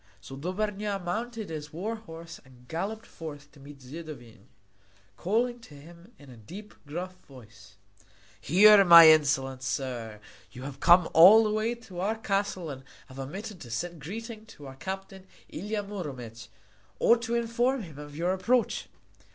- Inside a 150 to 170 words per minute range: Yes, average, 160 wpm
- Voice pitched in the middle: Yes, medium, 170 Hz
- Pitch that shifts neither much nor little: No, wide, 7.3 semitones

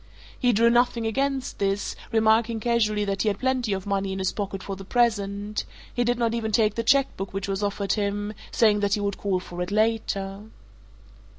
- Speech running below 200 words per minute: No, fast, 205 wpm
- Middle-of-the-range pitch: No, high, 210 Hz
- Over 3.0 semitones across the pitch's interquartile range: No, average, 2.7 semitones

